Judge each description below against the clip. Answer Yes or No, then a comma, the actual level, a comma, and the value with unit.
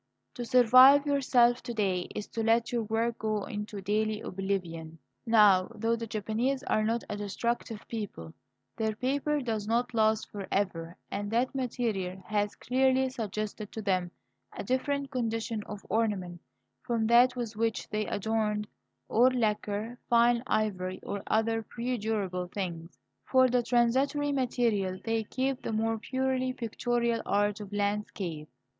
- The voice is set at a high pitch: Yes, high, 225 Hz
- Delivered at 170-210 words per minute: No, average, 145 wpm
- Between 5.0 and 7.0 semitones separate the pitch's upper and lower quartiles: No, average, 2.9 semitones